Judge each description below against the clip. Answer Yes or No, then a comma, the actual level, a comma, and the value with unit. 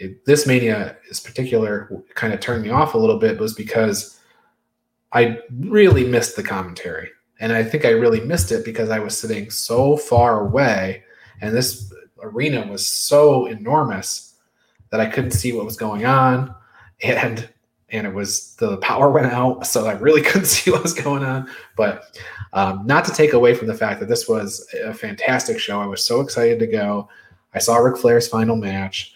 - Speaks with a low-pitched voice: Yes, low, 115 Hz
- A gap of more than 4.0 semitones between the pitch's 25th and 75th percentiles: Yes, average, 4.7 semitones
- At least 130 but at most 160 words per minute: No, average, 195 wpm